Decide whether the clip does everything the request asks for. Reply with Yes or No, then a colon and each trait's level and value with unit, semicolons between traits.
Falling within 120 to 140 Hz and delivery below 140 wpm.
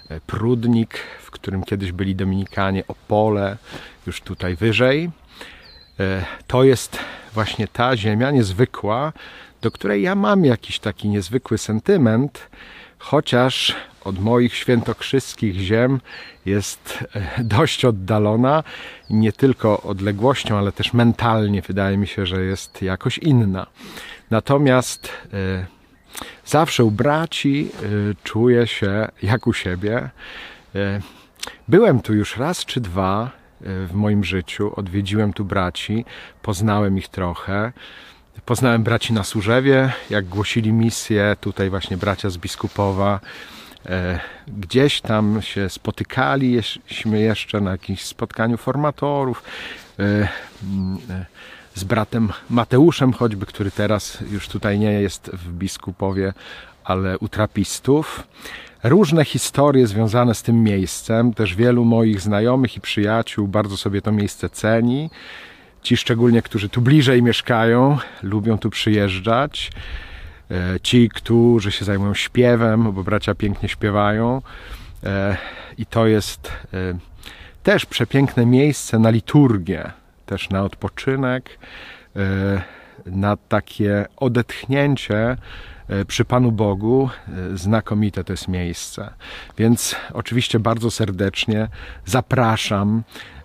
No: low, 105 Hz; slow, 110 wpm